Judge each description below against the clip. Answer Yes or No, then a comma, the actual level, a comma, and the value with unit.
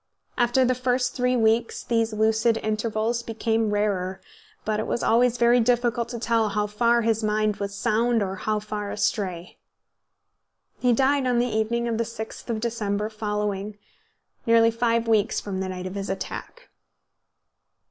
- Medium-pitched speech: No, high, 225 Hz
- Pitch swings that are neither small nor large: No, narrow, 2.2 semitones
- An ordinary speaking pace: Yes, average, 160 wpm